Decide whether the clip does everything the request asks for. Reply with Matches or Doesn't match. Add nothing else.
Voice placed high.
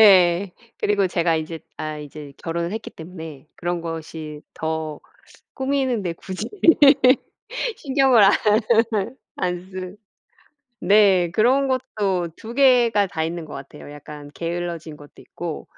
Doesn't match